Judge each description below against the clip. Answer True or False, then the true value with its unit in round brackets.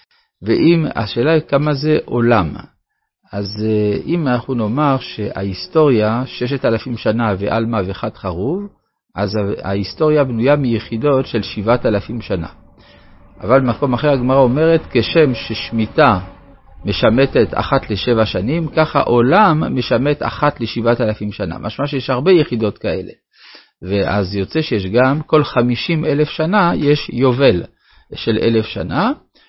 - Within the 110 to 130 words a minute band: True (125 wpm)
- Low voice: True (120 Hz)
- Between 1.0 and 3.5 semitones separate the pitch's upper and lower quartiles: False (5.5 semitones)